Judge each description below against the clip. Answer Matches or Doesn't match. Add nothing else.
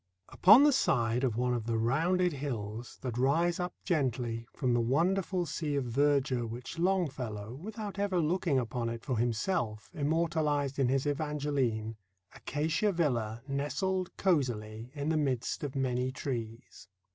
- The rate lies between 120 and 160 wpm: Matches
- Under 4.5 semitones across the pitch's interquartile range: Doesn't match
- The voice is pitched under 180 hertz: Matches